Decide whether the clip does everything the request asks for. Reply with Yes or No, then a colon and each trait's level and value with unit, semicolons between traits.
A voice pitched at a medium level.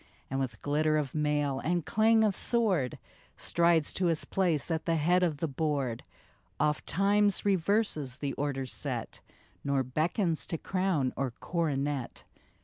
Yes: medium, 155 Hz